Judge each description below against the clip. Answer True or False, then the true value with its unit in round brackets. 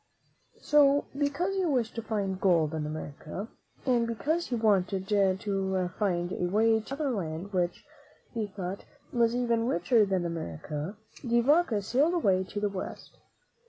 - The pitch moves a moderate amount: True (4.8 semitones)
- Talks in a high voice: True (205 Hz)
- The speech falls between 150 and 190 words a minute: True (155 wpm)